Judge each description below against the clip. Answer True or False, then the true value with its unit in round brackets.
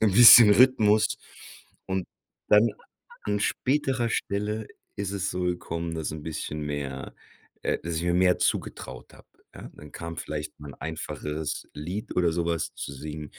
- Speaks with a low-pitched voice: True (85 Hz)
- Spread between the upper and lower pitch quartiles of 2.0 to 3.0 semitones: False (5.2 semitones)